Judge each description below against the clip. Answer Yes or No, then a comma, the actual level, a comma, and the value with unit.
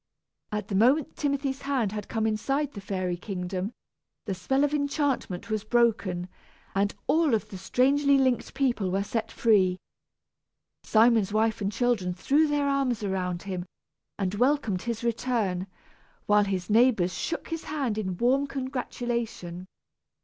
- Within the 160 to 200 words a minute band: No, average, 145 wpm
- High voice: Yes, high, 225 Hz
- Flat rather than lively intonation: No, wide, 5.6 semitones